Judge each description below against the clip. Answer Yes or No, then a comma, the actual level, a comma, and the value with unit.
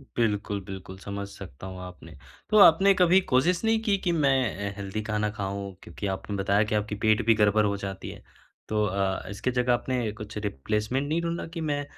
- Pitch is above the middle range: No, low, 105 Hz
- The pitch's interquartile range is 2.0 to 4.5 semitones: No, average, 4.9 semitones